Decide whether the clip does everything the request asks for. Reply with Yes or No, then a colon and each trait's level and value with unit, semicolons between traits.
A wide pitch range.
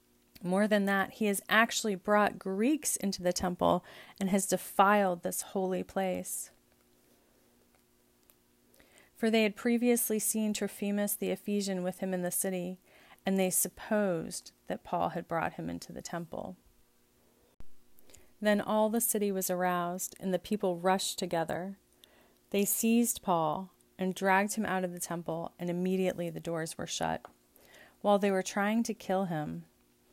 No: average, 3.5 semitones